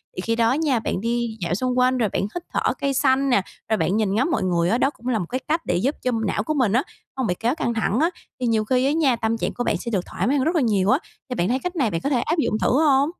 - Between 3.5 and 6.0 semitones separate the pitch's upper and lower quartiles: Yes, average, 4.1 semitones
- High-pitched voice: Yes, high, 245 Hz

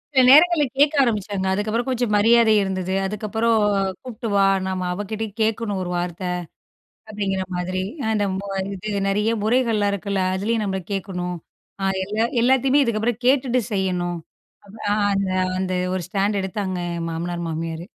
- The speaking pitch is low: No, high, 205 Hz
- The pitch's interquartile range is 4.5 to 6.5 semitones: No, average, 3.4 semitones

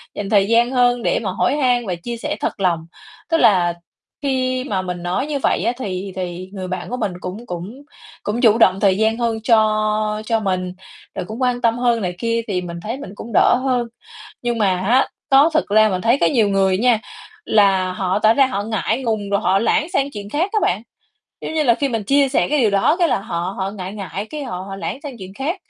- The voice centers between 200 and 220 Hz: Yes, high, 215 Hz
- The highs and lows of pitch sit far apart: No, average, 4.4 semitones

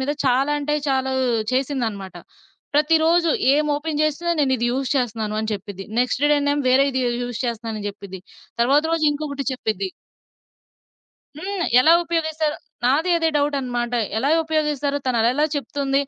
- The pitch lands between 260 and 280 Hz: Yes, very high, 275 Hz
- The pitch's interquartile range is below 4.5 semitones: Yes, average, 3.8 semitones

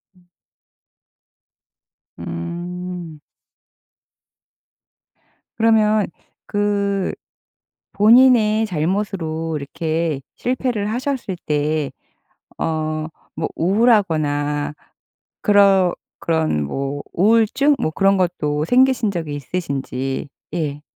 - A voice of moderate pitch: Yes, medium, 175 Hz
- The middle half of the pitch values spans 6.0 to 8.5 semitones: No, wide, 5.4 semitones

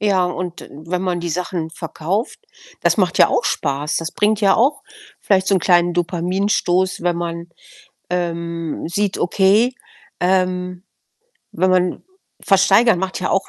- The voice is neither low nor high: Yes, medium, 180 Hz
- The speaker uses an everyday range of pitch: No, narrow, 2.1 semitones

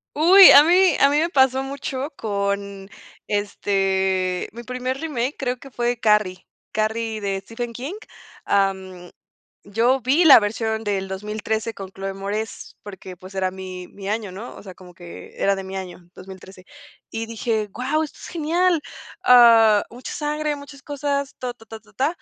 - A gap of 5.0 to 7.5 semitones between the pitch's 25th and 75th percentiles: Yes, wide, 5.5 semitones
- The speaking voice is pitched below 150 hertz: No, high, 220 Hz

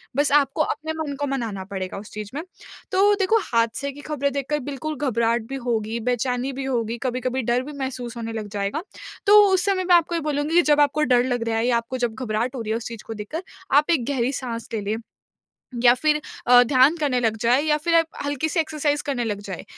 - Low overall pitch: No, very high, 255 Hz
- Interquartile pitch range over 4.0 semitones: Yes, average, 4.4 semitones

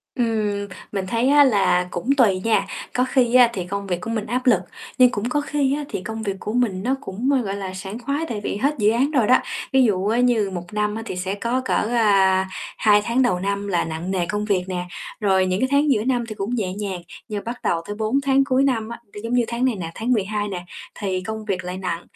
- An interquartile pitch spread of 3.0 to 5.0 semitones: Yes, average, 4.4 semitones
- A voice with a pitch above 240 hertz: No, high, 210 Hz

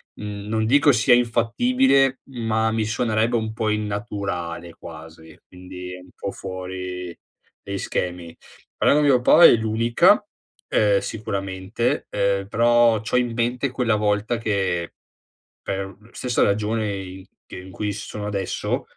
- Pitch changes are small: No, average, 3.6 semitones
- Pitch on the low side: Yes, low, 105 Hz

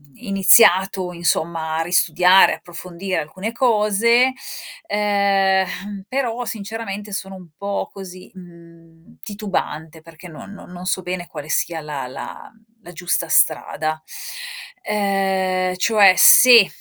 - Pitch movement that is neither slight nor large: Yes, average, 3.0 semitones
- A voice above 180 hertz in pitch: Yes, high, 190 Hz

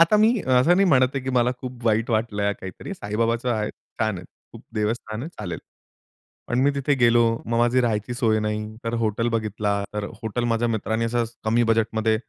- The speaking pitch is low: Yes, low, 115 Hz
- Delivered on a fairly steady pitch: Yes, narrow, 2.3 semitones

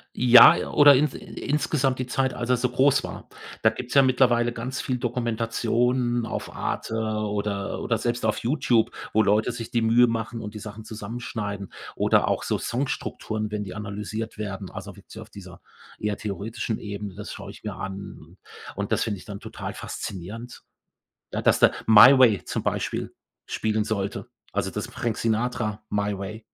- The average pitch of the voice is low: Yes, low, 110 Hz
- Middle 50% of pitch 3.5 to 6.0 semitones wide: No, average, 2.8 semitones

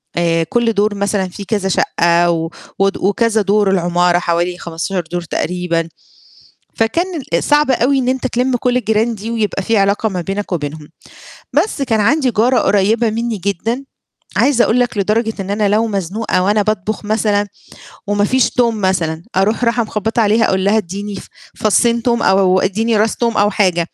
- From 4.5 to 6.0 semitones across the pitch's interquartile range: No, average, 3.5 semitones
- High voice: Yes, high, 205 Hz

